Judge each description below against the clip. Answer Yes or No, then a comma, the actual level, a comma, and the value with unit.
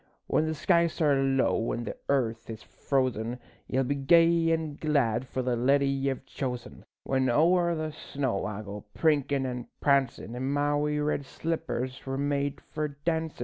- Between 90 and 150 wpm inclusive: No, average, 170 wpm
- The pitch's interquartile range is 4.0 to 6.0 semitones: No, average, 3.1 semitones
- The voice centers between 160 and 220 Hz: No, medium, 140 Hz